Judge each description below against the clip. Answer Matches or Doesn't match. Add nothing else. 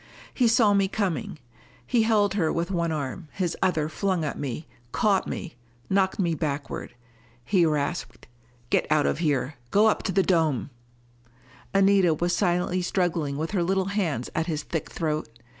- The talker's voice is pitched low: Doesn't match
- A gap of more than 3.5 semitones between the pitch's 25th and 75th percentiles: Matches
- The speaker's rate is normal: Matches